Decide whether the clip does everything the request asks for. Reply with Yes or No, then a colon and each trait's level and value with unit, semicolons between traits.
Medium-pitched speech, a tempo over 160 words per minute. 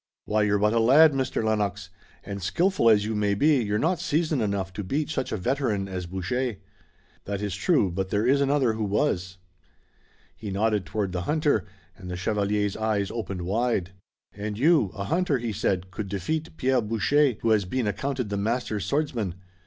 No: low, 105 Hz; average, 185 wpm